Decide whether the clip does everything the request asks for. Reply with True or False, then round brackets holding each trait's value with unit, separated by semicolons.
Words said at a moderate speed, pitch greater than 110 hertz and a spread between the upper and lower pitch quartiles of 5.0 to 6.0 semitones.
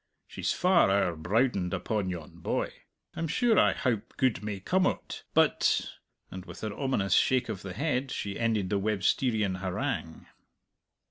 False (160 wpm; 105 Hz; 5.3 semitones)